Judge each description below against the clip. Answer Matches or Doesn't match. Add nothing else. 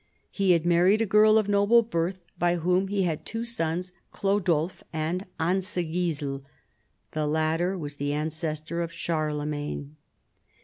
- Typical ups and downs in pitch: Matches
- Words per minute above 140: Doesn't match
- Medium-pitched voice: Matches